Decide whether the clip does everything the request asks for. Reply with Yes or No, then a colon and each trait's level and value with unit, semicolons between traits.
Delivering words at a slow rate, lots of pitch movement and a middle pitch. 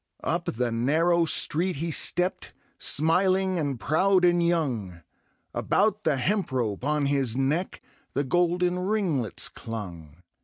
Yes: slow, 125 wpm; wide, 6.0 semitones; medium, 155 Hz